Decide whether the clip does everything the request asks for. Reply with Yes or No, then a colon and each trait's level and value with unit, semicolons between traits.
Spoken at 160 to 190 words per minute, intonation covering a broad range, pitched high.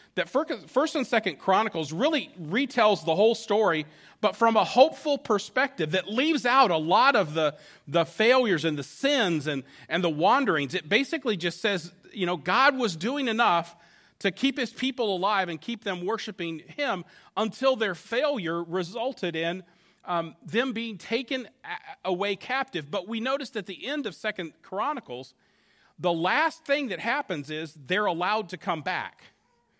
Yes: average, 165 wpm; wide, 6.8 semitones; high, 205 Hz